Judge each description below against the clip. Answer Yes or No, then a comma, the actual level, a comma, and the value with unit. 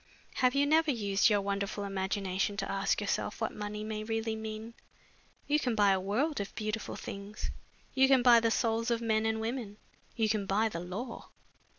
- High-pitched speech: Yes, high, 215 Hz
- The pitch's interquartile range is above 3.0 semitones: No, narrow, 2.5 semitones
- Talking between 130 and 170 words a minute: No, average, 190 wpm